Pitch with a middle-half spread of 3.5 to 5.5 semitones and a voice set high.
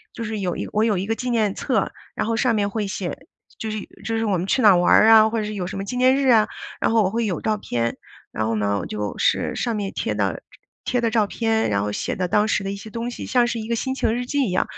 No: average, 3.1 semitones; high, 215 Hz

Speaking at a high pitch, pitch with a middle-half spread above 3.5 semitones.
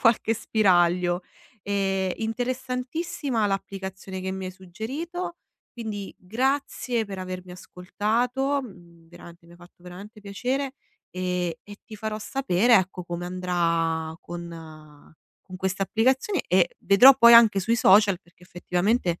Yes: high, 195 Hz; average, 4.7 semitones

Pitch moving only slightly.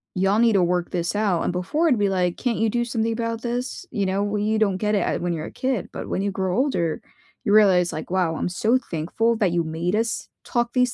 No: average, 4.3 semitones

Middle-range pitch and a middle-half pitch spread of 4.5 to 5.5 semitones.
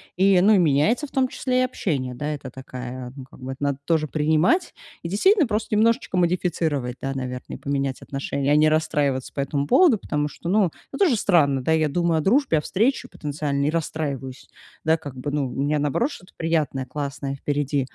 Yes: medium, 150 Hz; average, 4.8 semitones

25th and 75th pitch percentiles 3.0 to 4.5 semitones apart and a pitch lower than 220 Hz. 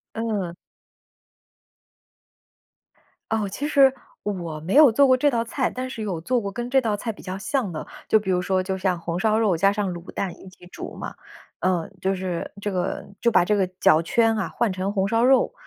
Yes: average, 4.0 semitones; high, 200 Hz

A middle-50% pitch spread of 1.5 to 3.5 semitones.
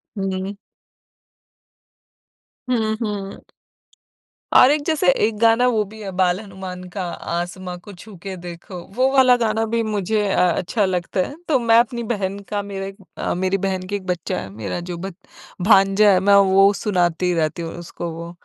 Yes: average, 3.2 semitones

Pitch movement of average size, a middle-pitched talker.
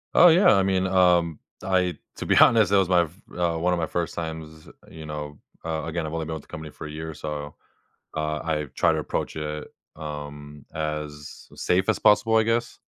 No: average, 3.2 semitones; very low, 80 Hz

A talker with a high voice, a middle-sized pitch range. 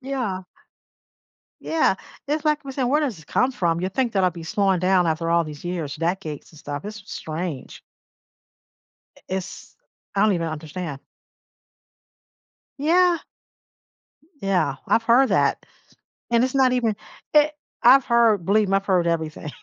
No: high, 195 Hz; wide, 7.0 semitones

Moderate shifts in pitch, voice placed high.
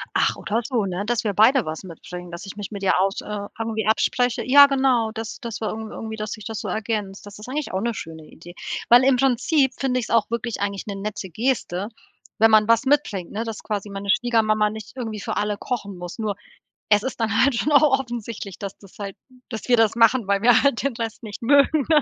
Yes: average, 3.2 semitones; high, 220 Hz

